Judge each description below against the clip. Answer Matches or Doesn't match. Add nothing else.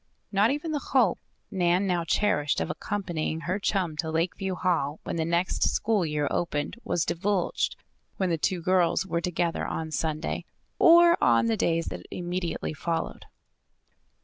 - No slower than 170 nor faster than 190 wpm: Doesn't match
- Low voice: Doesn't match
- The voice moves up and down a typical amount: Matches